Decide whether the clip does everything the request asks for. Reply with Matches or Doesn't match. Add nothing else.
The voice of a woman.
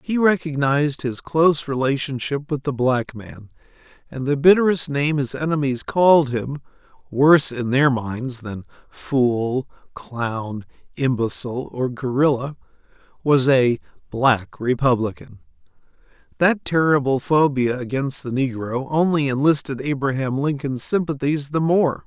Doesn't match